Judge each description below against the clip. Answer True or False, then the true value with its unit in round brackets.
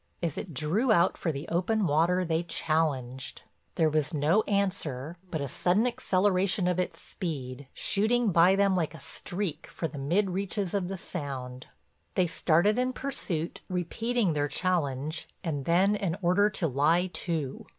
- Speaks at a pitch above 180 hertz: False (175 Hz)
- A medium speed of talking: True (160 wpm)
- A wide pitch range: False (4.3 semitones)